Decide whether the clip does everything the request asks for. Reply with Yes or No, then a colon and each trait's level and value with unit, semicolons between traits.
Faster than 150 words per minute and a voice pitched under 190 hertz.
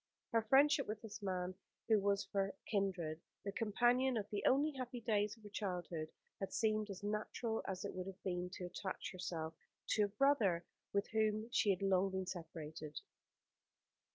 No: average, 180 wpm; high, 200 Hz